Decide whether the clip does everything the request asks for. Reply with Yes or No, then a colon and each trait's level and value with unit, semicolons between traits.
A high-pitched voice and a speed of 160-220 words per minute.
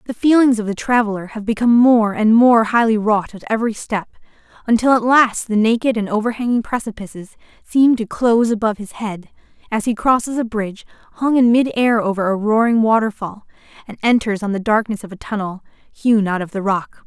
Yes: high, 220 Hz; average, 190 wpm